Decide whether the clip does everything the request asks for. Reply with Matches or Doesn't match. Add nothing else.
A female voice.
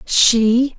Matches